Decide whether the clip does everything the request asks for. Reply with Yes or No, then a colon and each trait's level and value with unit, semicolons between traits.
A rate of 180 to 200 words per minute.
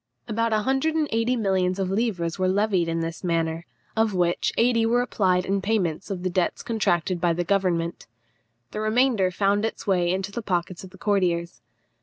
Yes: average, 190 wpm